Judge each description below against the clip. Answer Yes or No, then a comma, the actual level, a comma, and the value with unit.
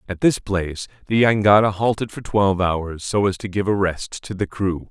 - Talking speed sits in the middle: No, fast, 220 wpm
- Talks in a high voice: No, low, 100 Hz